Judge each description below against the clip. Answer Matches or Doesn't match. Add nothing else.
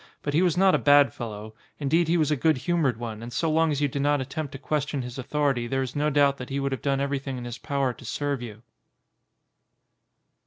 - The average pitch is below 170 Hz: Matches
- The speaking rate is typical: Doesn't match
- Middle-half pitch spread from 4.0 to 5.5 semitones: Doesn't match